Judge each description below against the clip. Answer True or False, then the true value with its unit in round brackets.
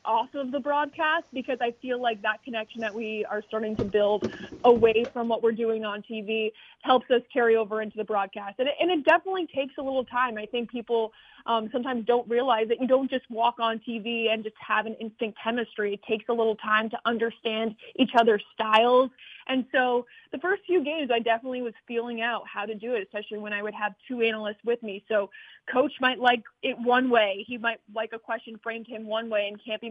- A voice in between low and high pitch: False (230 Hz)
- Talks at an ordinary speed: False (225 wpm)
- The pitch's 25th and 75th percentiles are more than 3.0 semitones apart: False (2.4 semitones)